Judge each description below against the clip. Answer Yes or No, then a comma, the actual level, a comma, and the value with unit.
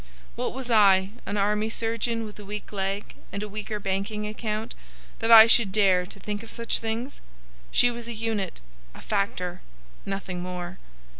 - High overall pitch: Yes, high, 210 Hz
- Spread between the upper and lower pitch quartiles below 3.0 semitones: Yes, narrow, 2.6 semitones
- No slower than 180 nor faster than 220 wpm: No, average, 165 wpm